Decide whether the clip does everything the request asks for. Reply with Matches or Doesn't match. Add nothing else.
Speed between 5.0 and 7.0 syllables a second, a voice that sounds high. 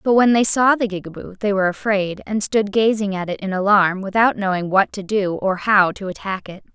Matches